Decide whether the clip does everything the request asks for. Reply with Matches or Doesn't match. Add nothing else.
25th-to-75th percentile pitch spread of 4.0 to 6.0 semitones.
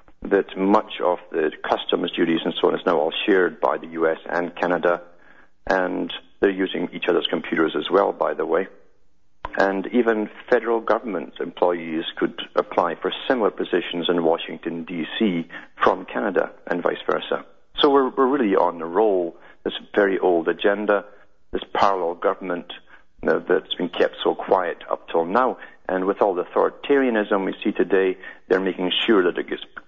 Doesn't match